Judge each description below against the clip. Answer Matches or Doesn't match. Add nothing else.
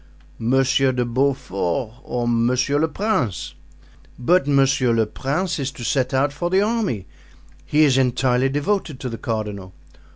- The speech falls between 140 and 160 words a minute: Matches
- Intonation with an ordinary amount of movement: Matches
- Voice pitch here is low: Matches